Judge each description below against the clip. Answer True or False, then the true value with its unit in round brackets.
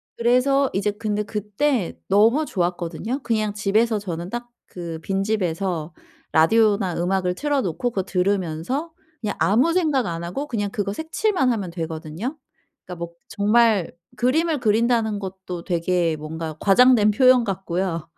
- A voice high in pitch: True (205 Hz)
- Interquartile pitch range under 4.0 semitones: False (5.2 semitones)